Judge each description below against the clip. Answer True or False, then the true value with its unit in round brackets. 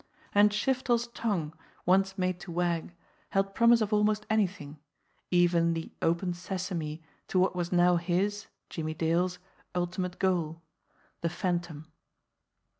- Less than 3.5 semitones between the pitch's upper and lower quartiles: True (2.7 semitones)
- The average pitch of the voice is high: False (180 Hz)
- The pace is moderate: False (130 wpm)